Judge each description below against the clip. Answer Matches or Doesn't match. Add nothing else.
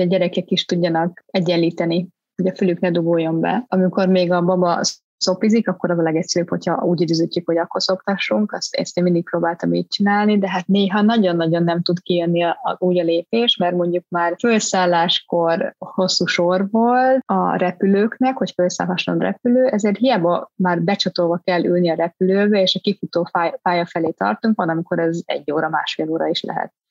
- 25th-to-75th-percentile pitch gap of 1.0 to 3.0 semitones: Matches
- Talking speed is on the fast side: Matches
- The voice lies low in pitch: Doesn't match